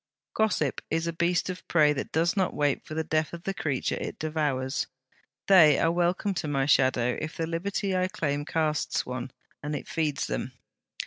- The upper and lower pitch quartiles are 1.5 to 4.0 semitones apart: Yes, average, 2.9 semitones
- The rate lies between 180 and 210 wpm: Yes, average, 190 wpm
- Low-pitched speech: No, medium, 155 Hz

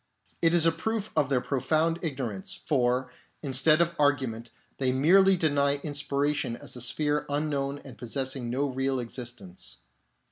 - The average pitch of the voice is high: No, medium, 140 Hz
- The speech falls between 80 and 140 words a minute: No, average, 180 wpm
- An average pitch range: Yes, average, 3.5 semitones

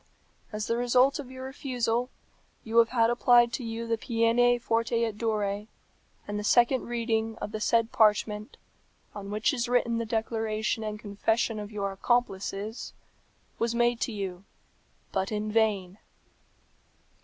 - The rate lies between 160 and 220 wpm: No, average, 150 wpm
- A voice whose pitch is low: No, high, 225 Hz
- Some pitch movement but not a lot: No, narrow, 2.1 semitones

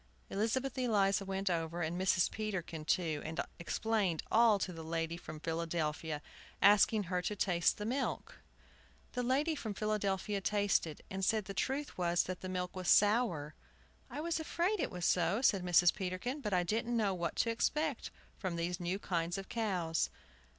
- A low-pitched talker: No, high, 190 Hz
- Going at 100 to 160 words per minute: No, average, 170 wpm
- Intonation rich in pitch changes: No, average, 4.3 semitones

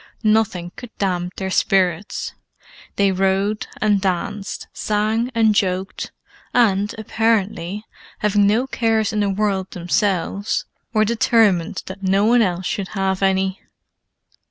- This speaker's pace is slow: Yes, slow, 125 wpm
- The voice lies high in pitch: Yes, high, 200 Hz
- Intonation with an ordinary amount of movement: No, narrow, 2.2 semitones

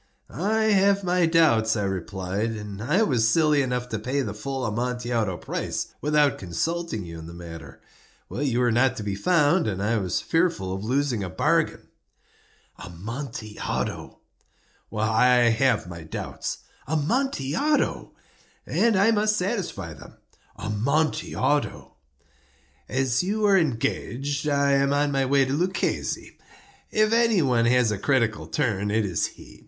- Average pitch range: No, wide, 6.9 semitones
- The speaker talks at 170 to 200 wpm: No, average, 140 wpm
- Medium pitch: No, low, 130 Hz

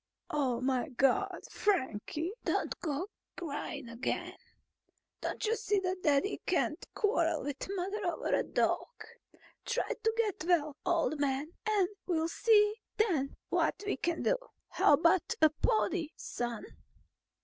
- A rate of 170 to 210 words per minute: No, average, 140 wpm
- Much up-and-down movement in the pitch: Yes, wide, 5.9 semitones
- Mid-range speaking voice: No, very high, 335 Hz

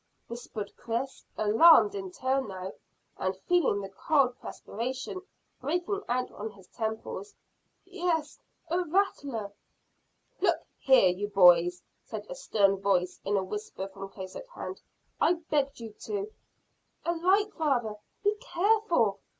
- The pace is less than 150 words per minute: Yes, slow, 135 wpm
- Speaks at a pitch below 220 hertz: No, very high, 255 Hz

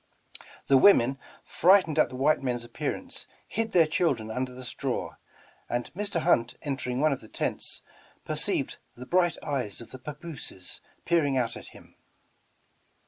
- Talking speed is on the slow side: No, average, 155 wpm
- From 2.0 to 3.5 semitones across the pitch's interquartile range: No, average, 5.0 semitones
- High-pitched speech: No, low, 135 Hz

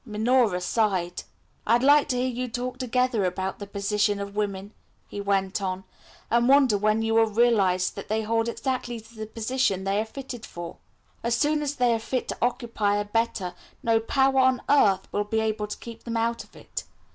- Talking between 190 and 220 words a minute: Yes, average, 195 wpm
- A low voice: No, high, 225 Hz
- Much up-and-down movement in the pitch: No, average, 3.3 semitones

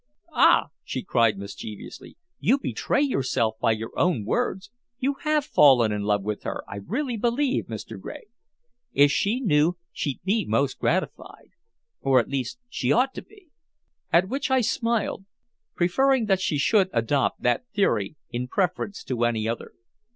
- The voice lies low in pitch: No, medium, 175 Hz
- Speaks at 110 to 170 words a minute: Yes, average, 160 wpm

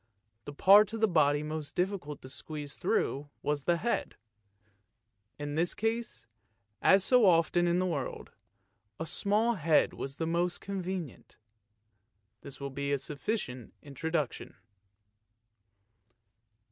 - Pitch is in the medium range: Yes, medium, 165 Hz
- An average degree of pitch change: Yes, average, 4.9 semitones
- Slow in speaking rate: Yes, slow, 125 wpm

